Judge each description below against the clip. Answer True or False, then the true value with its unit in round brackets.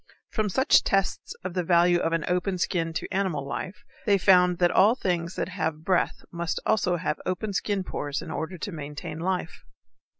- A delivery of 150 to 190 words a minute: True (185 wpm)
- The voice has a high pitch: False (180 Hz)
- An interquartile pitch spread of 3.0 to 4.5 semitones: False (2.5 semitones)